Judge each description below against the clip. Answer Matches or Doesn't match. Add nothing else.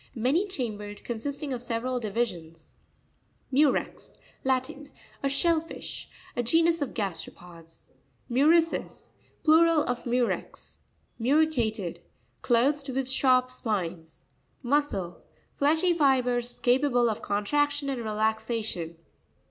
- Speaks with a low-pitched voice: Doesn't match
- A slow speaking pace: Matches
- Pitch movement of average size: Matches